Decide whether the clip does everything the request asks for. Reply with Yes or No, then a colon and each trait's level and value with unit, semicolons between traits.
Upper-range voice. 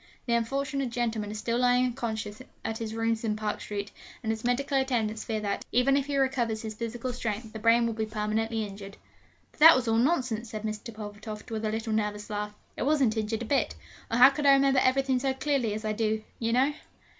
Yes: high, 225 Hz